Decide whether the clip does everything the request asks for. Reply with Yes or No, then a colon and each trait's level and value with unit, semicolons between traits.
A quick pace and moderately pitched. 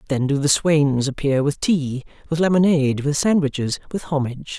No: average, 170 wpm; medium, 145 Hz